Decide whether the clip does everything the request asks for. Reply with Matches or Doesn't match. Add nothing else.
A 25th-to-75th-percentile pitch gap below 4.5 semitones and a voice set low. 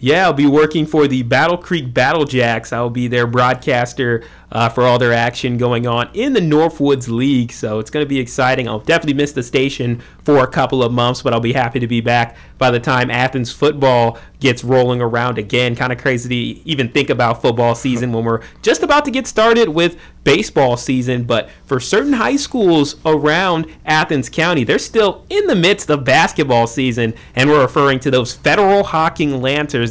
Matches